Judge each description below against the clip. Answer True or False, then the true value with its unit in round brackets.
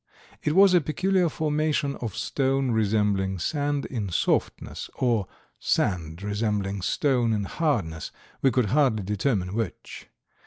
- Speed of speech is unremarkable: False (125 wpm)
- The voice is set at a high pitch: False (115 Hz)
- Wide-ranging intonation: True (6.3 semitones)